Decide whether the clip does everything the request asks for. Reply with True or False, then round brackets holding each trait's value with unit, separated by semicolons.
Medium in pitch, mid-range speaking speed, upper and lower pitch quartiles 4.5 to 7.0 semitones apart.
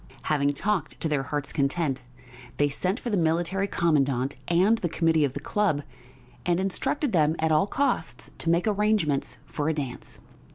True (160 Hz; 170 wpm; 4.9 semitones)